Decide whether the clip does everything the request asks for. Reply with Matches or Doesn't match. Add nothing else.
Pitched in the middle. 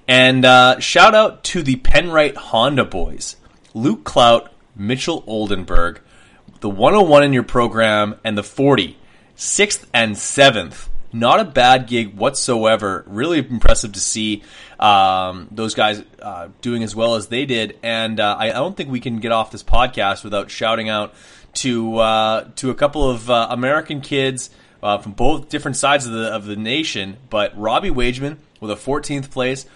Doesn't match